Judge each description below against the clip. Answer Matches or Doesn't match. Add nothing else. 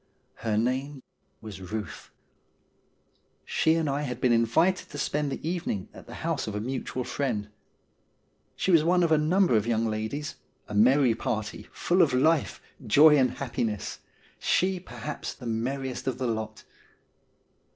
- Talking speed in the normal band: Matches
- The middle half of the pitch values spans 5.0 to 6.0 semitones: Matches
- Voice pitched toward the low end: Matches